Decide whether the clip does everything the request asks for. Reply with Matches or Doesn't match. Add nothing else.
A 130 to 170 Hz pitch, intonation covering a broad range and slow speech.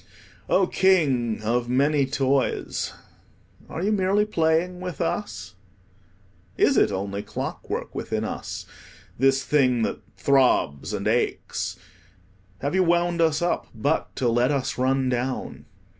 Matches